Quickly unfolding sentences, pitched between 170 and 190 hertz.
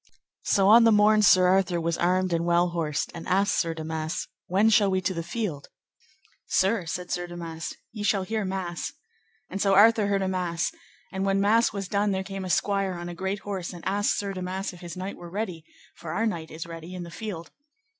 Yes: fast, 215 wpm; medium, 185 Hz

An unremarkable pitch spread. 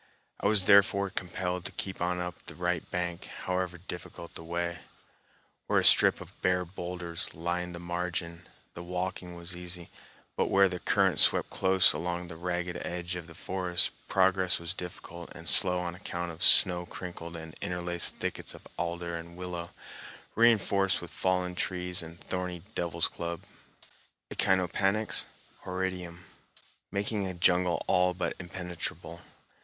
No: narrow, 1.0 semitones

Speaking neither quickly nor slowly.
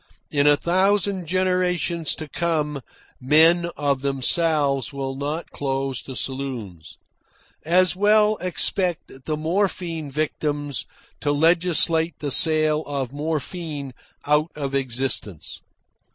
No: slow, 110 wpm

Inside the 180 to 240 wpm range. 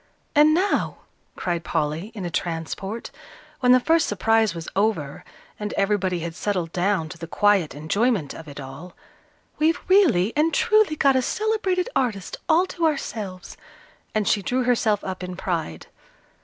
No: average, 155 wpm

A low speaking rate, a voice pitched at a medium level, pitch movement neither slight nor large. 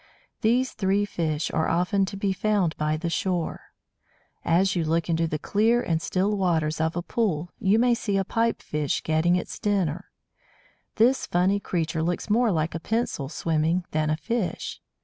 No: average, 175 wpm; medium, 180 Hz; average, 4.3 semitones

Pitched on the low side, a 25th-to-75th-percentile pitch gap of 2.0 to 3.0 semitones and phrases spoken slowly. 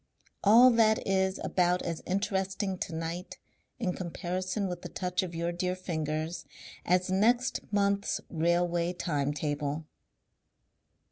No: medium, 180 Hz; narrow, 2.4 semitones; slow, 125 wpm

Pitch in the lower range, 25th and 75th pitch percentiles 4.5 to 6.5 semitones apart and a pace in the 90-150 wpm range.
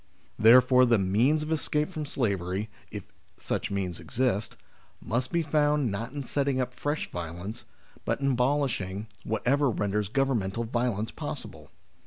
Yes: low, 125 Hz; wide, 5.4 semitones; average, 145 wpm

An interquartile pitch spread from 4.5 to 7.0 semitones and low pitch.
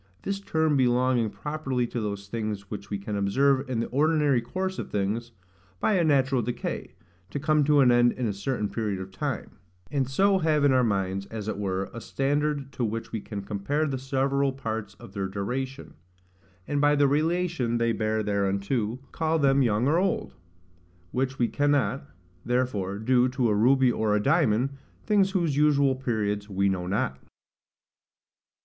Yes: average, 5.3 semitones; low, 125 Hz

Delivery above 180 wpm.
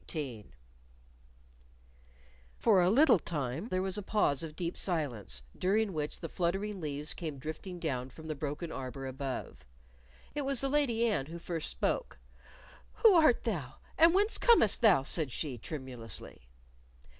No: average, 155 wpm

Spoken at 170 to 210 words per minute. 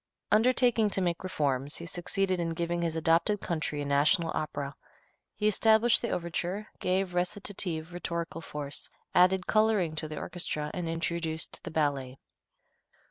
No: average, 140 wpm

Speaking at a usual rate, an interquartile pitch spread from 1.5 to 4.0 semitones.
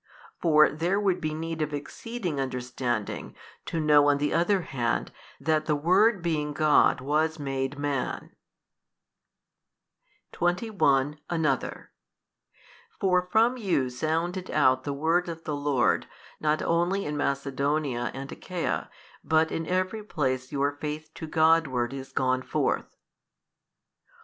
No: slow, 125 wpm; average, 3.7 semitones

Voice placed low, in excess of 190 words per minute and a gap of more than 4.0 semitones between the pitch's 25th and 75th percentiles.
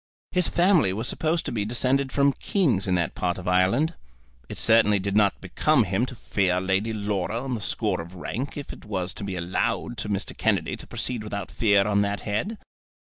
Yes: low, 105 Hz; fast, 205 wpm; average, 4.8 semitones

